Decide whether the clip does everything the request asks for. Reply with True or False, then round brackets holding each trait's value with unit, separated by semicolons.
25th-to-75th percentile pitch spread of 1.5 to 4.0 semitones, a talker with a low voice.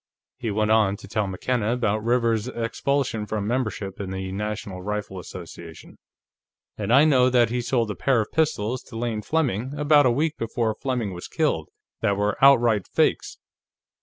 True (3.5 semitones; 115 Hz)